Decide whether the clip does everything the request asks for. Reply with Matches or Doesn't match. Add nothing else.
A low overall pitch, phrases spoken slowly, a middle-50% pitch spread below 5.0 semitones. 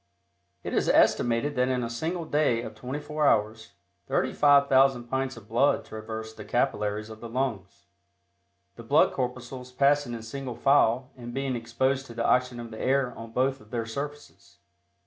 Doesn't match